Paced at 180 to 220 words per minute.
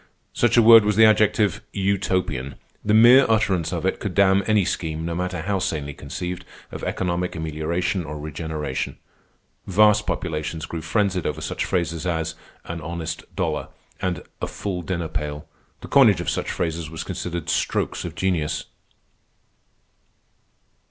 No: average, 150 wpm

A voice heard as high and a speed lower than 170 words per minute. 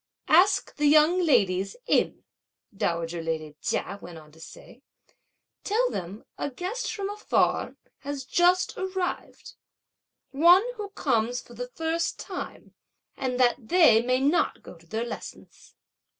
Yes: very high, 265 Hz; slow, 135 wpm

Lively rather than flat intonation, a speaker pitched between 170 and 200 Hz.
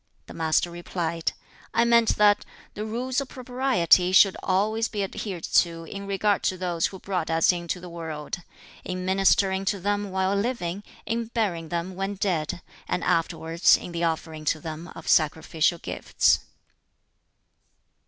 No: average, 3.4 semitones; medium, 185 Hz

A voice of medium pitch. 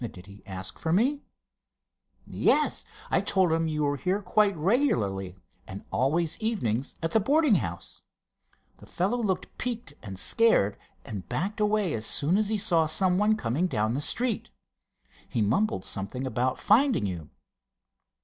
Yes: medium, 165 Hz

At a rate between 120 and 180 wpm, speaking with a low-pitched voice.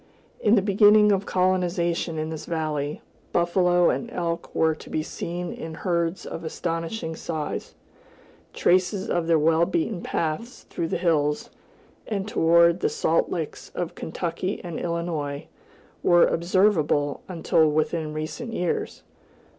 No: slow, 135 wpm; medium, 170 Hz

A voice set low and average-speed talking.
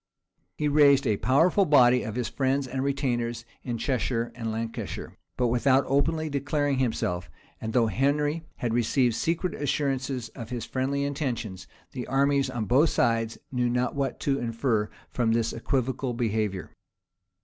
Yes: low, 130 Hz; average, 150 wpm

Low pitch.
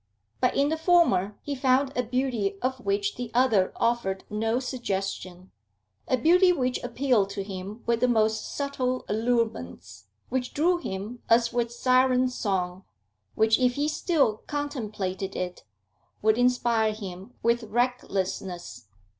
No: high, 235 Hz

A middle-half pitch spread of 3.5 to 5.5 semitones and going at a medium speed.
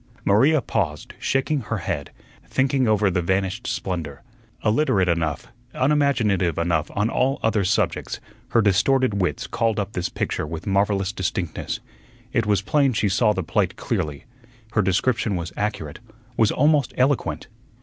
Yes: average, 5.1 semitones; average, 145 wpm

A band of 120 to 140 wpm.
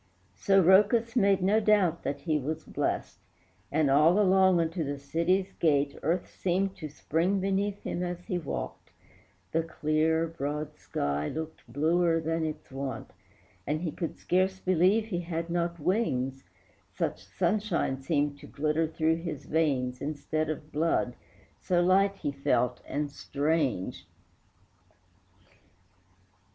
Yes: slow, 135 wpm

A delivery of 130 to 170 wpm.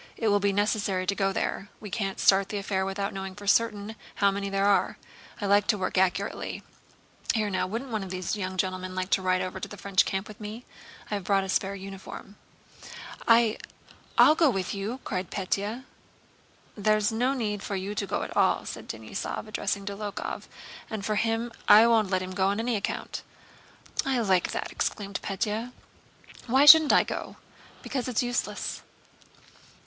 No: average, 185 wpm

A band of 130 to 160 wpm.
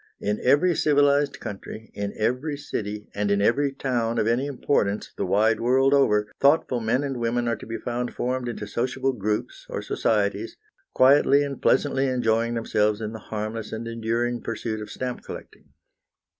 No: average, 170 wpm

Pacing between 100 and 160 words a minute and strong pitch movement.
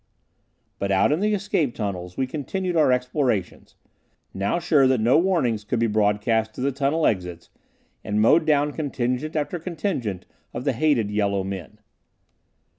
Yes: average, 155 wpm; wide, 6.8 semitones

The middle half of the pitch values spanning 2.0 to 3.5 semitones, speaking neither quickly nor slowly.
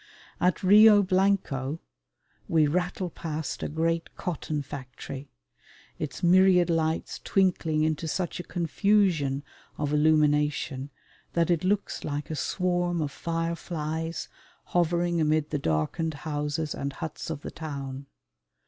No: average, 3.1 semitones; slow, 120 wpm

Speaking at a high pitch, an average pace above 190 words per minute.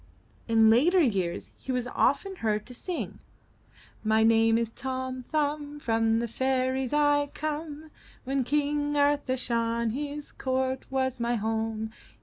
No: very high, 260 Hz; slow, 135 wpm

